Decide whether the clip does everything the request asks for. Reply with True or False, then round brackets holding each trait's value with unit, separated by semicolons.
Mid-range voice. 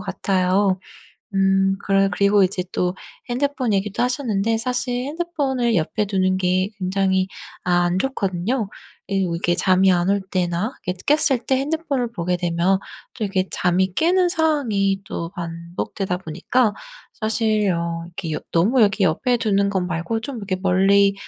False (195 Hz)